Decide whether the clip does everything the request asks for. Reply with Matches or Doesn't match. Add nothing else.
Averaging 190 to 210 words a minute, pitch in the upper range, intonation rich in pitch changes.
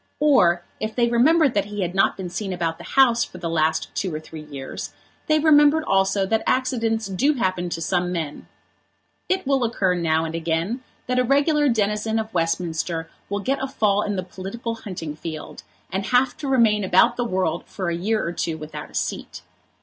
Matches